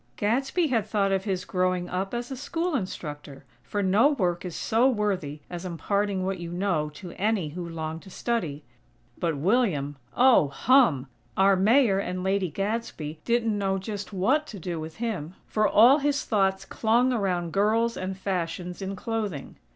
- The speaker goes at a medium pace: Yes, average, 170 wpm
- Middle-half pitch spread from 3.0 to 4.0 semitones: No, average, 4.4 semitones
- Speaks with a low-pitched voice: No, high, 195 Hz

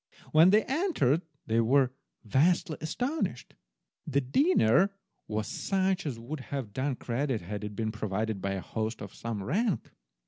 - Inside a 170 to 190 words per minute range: No, average, 150 wpm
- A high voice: No, low, 130 Hz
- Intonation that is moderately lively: No, wide, 8.2 semitones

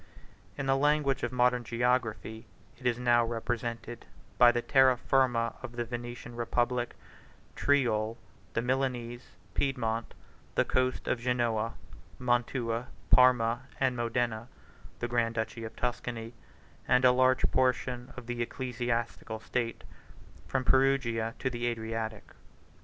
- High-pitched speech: No, low, 120 Hz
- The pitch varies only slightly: Yes, narrow, 1.6 semitones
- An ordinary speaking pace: No, slow, 125 wpm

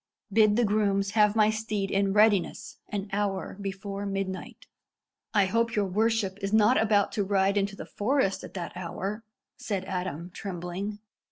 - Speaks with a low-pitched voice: No, high, 200 Hz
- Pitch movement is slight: Yes, narrow, 1.7 semitones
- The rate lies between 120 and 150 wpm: No, average, 160 wpm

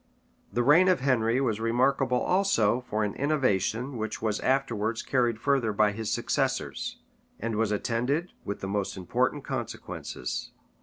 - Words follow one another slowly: No, average, 145 wpm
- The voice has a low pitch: Yes, low, 115 Hz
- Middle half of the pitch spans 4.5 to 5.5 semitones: No, average, 4.1 semitones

